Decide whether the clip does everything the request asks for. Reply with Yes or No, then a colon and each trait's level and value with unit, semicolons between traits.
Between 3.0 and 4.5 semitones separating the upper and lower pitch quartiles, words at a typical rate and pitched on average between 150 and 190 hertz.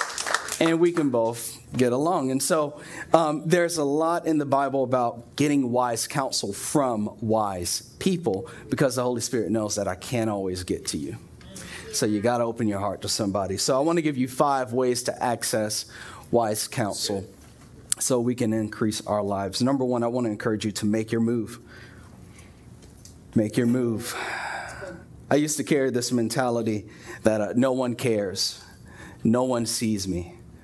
No: average, 3.5 semitones; average, 175 wpm; low, 120 Hz